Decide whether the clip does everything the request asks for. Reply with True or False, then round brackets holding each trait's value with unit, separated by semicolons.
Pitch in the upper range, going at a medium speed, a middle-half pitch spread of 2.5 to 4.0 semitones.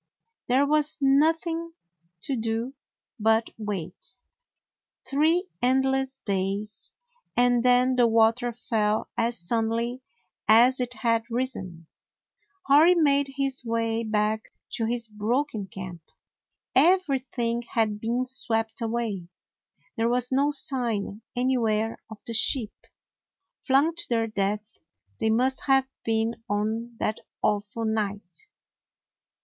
False (235 Hz; 120 wpm; 3.3 semitones)